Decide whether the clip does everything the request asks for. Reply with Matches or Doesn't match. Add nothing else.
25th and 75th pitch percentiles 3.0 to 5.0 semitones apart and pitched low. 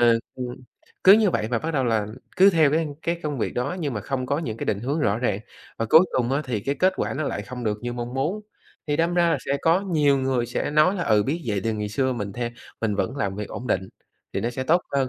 Doesn't match